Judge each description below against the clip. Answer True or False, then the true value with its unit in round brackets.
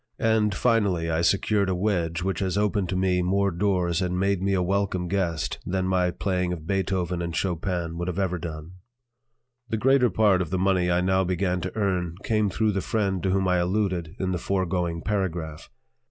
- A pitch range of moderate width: False (2.0 semitones)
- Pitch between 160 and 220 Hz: False (95 Hz)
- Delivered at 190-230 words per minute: True (195 wpm)